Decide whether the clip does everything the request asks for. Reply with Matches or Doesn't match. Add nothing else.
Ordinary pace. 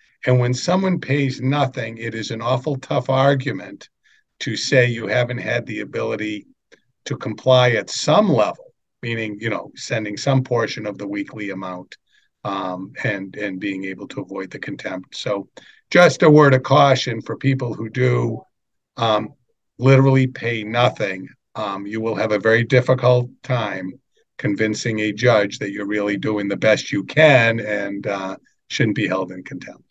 Matches